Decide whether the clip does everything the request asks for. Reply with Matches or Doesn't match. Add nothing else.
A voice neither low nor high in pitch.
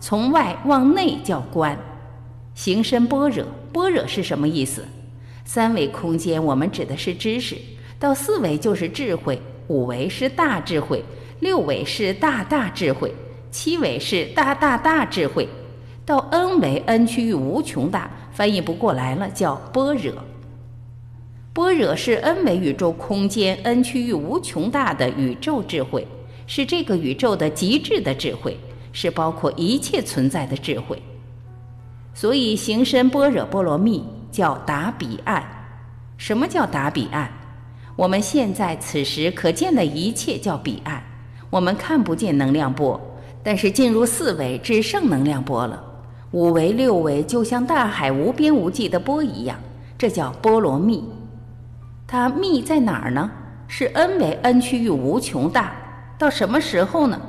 Matches